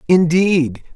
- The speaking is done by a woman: No, male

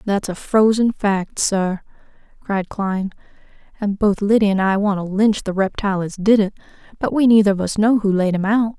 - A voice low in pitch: No, high, 205 Hz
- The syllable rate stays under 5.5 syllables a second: Yes, 5.2 syllables/s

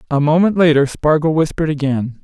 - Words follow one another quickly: No, average, 160 wpm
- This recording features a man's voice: Yes, male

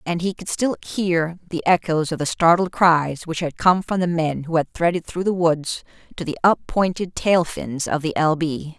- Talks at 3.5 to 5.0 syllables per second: Yes, 4.7 syllables/s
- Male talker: No, female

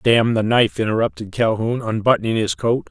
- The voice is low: Yes, low, 115 Hz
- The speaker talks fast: No, average, 165 wpm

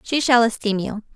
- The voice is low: No, high, 230 Hz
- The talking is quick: Yes, fast, 210 wpm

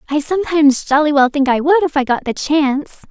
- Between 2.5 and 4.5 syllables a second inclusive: No, 6.1 syllables/s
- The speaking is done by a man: No, female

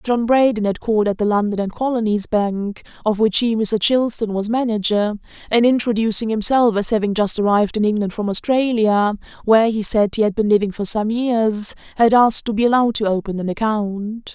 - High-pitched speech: Yes, high, 215 Hz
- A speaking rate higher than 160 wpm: Yes, average, 195 wpm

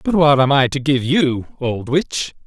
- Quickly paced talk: Yes, fast, 220 wpm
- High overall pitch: No, medium, 140 Hz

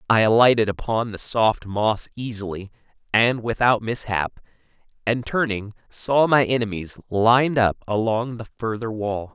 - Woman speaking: No, male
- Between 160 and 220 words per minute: No, slow, 135 wpm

